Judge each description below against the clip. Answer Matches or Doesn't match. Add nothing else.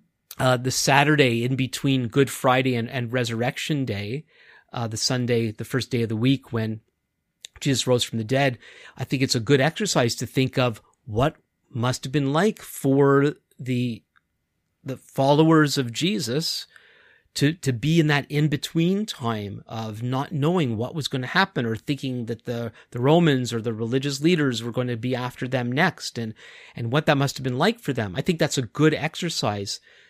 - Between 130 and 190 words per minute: Matches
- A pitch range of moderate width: Matches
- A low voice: Matches